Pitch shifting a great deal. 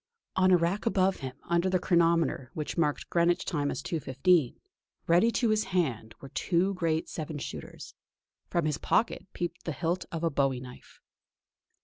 No: average, 4.0 semitones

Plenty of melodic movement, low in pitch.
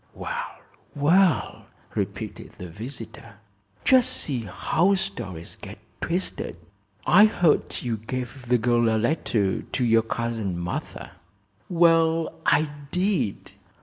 Yes: wide, 6.9 semitones; low, 125 Hz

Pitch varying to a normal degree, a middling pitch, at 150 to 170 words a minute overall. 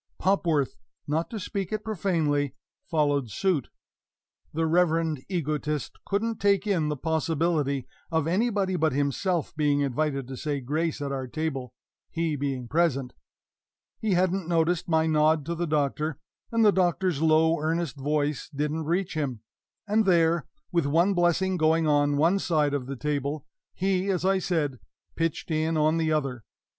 Yes: average, 3.3 semitones; medium, 160 Hz; average, 155 wpm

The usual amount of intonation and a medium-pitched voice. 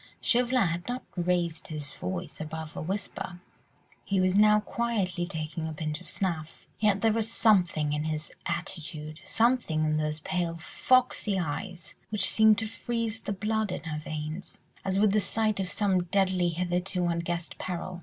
Yes: average, 4.6 semitones; medium, 180 Hz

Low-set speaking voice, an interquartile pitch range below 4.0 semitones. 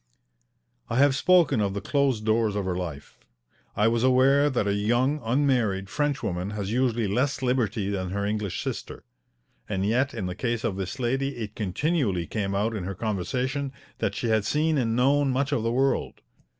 No: low, 115 Hz; average, 4.7 semitones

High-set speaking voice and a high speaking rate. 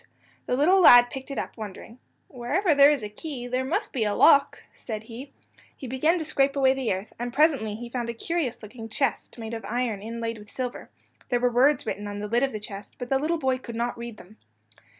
Yes: high, 245 Hz; fast, 230 wpm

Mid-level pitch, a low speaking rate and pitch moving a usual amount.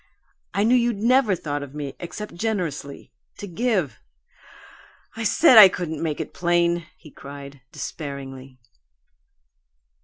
No: medium, 170 Hz; slow, 125 wpm; wide, 6.7 semitones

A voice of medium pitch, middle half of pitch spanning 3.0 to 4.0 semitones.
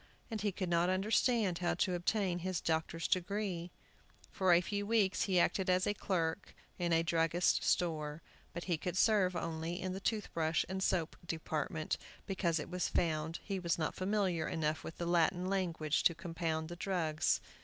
No: medium, 175 Hz; narrow, 2.5 semitones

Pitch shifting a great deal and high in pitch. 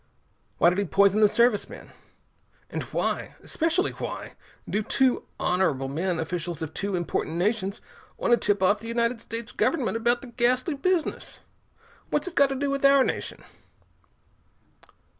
Yes: wide, 5.7 semitones; high, 225 Hz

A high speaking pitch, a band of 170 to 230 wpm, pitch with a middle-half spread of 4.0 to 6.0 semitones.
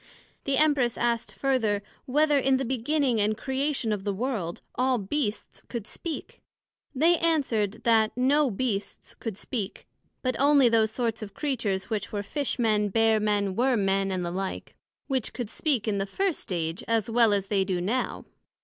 Yes: high, 230 Hz; average, 175 wpm; average, 4.5 semitones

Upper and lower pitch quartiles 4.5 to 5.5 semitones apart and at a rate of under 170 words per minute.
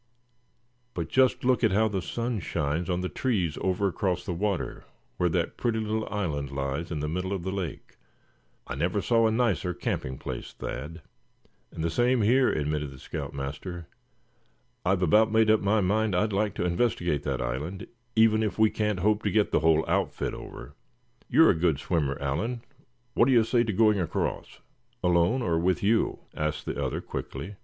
No: average, 5.1 semitones; average, 185 wpm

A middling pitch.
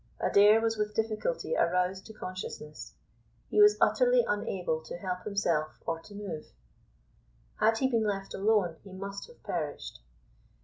No: high, 200 Hz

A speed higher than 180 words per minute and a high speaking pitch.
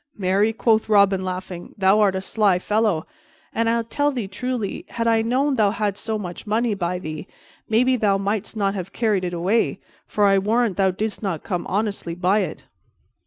Yes: average, 190 wpm; high, 205 Hz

